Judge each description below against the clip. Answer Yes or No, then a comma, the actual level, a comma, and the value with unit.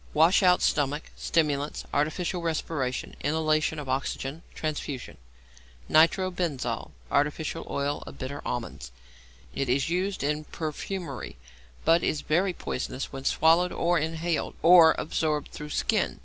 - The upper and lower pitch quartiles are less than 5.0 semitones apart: Yes, average, 2.9 semitones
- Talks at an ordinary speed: No, slow, 130 wpm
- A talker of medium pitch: Yes, medium, 155 Hz